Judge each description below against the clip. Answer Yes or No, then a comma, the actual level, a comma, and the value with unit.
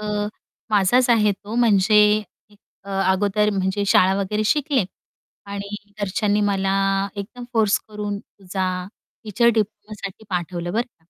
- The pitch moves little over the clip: Yes, narrow, 1.8 semitones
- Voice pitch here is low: No, high, 205 Hz